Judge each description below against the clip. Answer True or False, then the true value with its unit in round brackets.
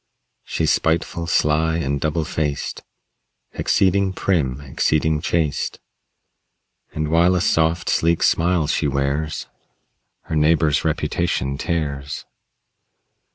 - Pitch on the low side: True (80 Hz)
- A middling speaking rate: False (100 wpm)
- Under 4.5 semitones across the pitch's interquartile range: True (2.4 semitones)